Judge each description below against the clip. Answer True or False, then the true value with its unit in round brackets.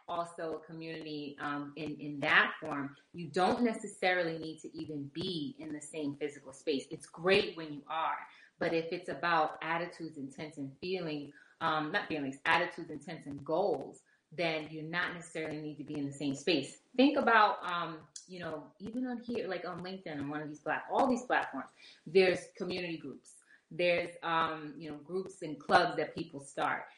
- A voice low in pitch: False (160 Hz)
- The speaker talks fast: False (190 wpm)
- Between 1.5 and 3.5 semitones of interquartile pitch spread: True (2.8 semitones)